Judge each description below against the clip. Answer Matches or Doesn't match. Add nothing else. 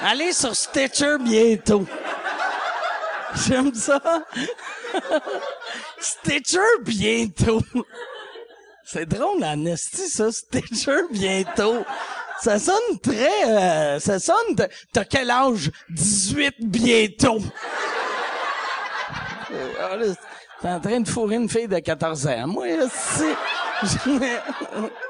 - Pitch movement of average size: Doesn't match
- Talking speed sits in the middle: Doesn't match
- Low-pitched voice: Doesn't match